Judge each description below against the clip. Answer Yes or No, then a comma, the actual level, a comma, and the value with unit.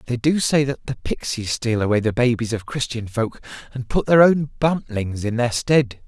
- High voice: No, low, 125 Hz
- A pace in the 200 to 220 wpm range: Yes, fast, 205 wpm